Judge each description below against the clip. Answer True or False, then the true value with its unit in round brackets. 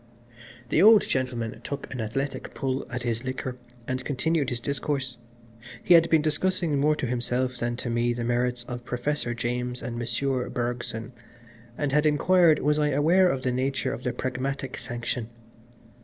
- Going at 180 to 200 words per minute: False (170 wpm)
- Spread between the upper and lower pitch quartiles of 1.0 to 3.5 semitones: True (3.2 semitones)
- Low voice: True (130 Hz)